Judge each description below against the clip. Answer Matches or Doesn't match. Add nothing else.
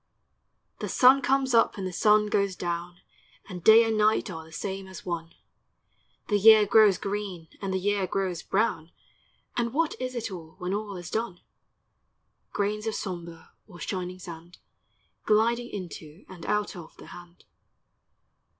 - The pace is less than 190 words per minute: Matches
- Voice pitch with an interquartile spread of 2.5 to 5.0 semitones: Matches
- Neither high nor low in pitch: Doesn't match